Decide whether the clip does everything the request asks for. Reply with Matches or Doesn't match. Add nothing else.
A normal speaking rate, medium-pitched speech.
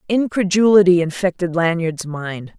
Doesn't match